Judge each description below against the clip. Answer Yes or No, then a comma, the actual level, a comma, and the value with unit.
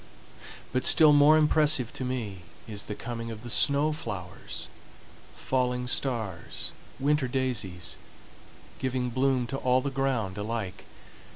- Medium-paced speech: No, slow, 115 wpm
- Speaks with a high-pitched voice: No, low, 125 Hz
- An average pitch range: Yes, average, 3.6 semitones